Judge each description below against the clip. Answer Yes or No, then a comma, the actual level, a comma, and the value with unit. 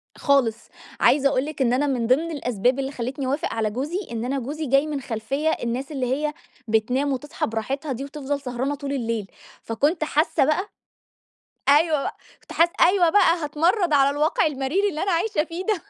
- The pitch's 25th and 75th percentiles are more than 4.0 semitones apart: No, average, 3.4 semitones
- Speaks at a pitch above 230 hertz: Yes, very high, 280 Hz